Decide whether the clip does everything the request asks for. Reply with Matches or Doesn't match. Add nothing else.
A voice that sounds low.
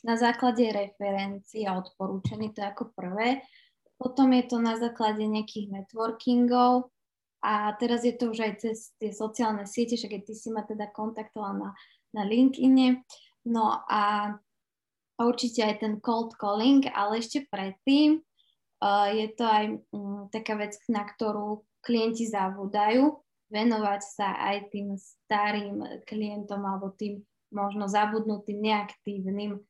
Doesn't match